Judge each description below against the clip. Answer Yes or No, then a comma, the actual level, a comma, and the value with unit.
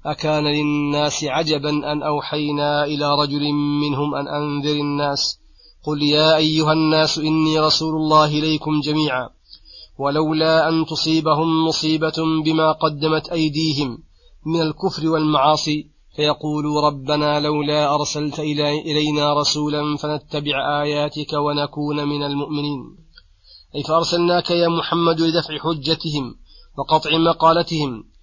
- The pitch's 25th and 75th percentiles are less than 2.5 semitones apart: Yes, narrow, 1.2 semitones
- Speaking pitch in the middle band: Yes, medium, 150 Hz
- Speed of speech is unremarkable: Yes, average, 105 wpm